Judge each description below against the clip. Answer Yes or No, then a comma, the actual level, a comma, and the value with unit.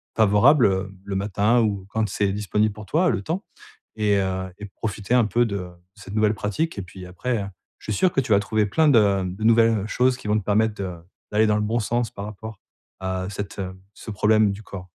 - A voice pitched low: Yes, low, 105 Hz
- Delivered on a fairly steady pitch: Yes, narrow, 2.2 semitones